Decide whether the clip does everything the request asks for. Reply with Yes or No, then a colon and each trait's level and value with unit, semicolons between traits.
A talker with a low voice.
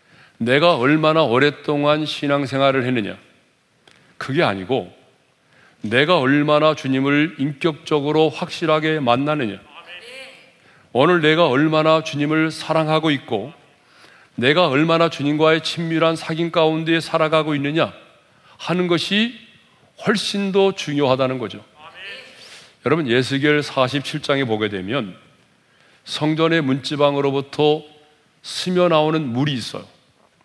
No: medium, 155 Hz